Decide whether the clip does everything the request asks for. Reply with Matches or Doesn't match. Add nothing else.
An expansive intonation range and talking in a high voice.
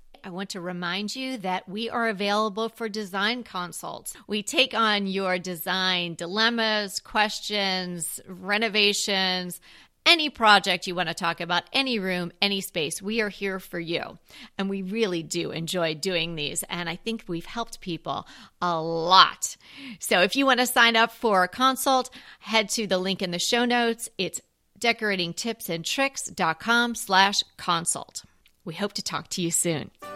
Doesn't match